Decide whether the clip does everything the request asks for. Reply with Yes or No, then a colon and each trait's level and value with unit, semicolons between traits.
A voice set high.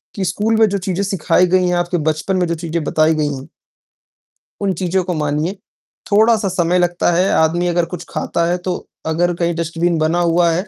No: medium, 175 Hz